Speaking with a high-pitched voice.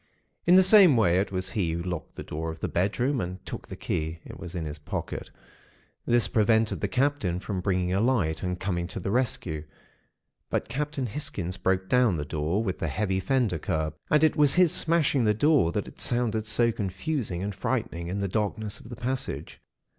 No: low, 100 Hz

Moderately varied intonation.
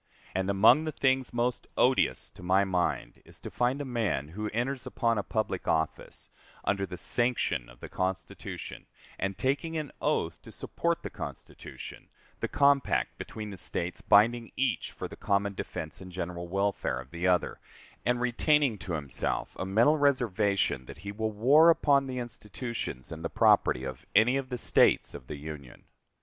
No: wide, 5.9 semitones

